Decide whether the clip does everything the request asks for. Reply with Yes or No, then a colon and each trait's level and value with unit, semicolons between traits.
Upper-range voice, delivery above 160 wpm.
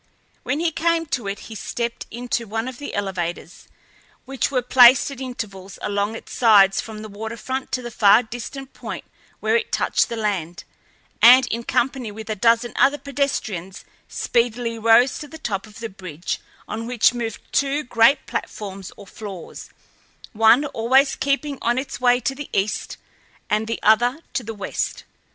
Yes: high, 230 Hz; average, 170 wpm